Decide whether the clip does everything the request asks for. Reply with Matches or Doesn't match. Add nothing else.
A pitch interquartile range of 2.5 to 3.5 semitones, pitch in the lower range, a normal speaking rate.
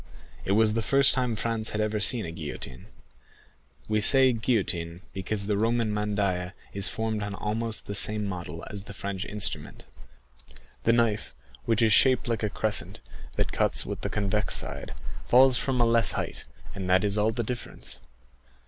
Matches